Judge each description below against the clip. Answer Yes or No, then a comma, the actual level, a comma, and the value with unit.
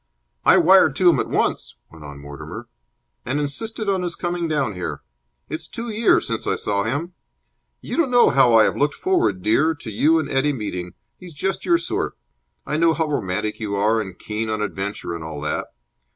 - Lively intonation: Yes, wide, 8.8 semitones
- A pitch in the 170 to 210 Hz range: No, low, 135 Hz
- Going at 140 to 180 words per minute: No, fast, 205 wpm